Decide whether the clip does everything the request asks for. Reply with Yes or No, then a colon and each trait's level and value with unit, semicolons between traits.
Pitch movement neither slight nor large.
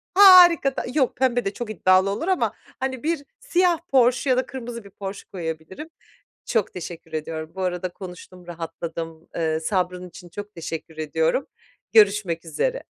No: wide, 7.6 semitones